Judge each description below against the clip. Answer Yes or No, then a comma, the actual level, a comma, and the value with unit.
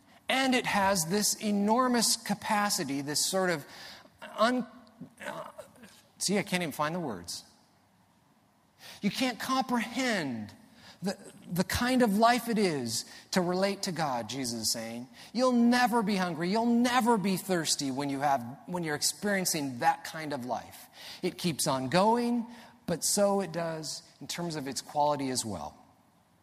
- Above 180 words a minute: No, average, 155 wpm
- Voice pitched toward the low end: No, medium, 185 Hz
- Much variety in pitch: Yes, wide, 7.0 semitones